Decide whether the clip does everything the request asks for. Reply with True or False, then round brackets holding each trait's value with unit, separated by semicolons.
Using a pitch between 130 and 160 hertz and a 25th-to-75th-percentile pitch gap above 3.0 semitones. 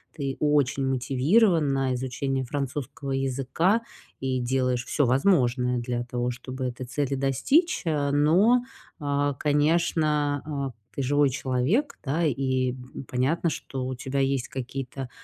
False (135 Hz; 2.5 semitones)